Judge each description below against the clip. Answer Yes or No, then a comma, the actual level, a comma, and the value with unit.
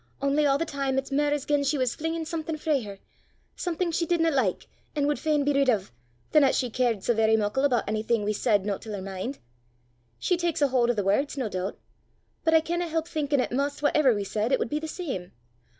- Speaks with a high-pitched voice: Yes, very high, 275 Hz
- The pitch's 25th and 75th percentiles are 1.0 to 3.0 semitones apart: No, wide, 5.6 semitones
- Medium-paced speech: No, fast, 240 wpm